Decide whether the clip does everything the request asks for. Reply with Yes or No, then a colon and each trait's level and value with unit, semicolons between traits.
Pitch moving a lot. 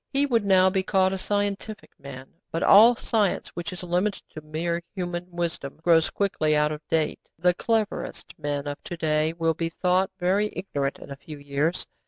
No: average, 4.0 semitones